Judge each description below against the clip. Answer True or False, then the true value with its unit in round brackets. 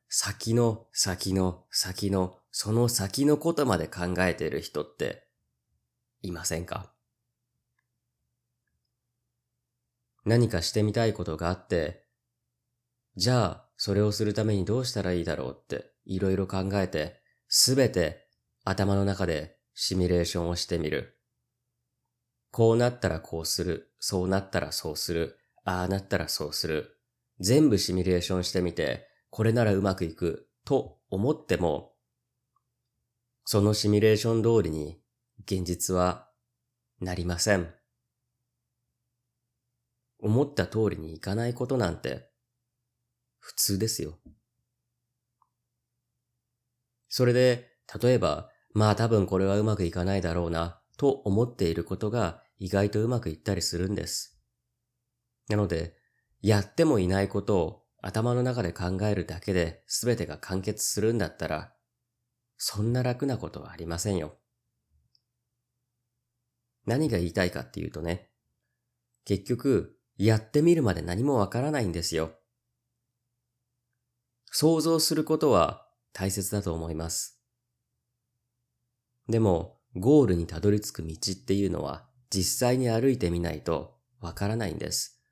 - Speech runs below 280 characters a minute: True (260 characters per minute)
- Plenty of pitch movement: False (4.8 semitones)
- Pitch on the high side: False (110 Hz)